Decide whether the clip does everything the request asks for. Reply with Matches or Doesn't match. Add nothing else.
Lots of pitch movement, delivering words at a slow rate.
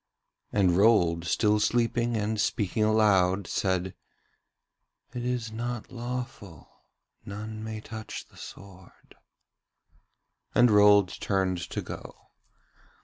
Doesn't match